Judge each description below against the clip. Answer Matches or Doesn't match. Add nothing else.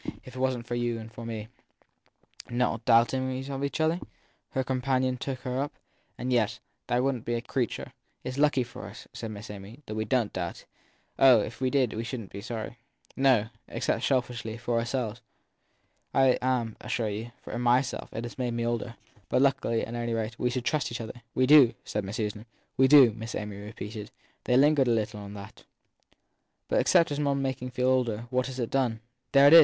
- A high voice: Doesn't match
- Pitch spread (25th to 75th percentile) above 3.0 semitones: Doesn't match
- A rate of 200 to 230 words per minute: Matches